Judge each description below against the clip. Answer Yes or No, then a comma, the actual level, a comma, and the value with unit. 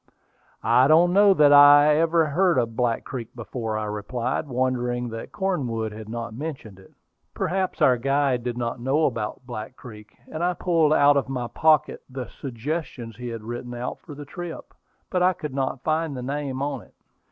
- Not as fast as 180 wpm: No, average, 185 wpm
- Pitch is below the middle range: Yes, low, 130 Hz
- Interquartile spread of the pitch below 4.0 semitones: No, average, 4.3 semitones